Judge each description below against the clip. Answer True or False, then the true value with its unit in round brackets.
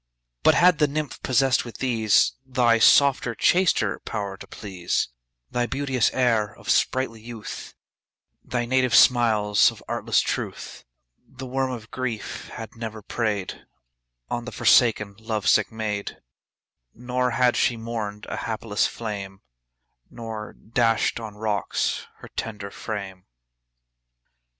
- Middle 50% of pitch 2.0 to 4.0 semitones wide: True (3.0 semitones)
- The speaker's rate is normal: False (130 wpm)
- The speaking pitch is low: True (115 Hz)